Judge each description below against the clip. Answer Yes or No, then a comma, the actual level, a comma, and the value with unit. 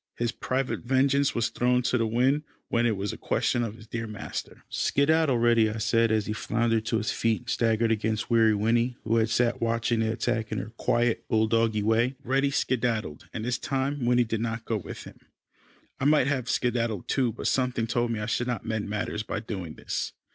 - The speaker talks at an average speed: No, fast, 210 wpm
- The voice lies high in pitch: No, low, 115 Hz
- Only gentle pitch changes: Yes, narrow, 1.9 semitones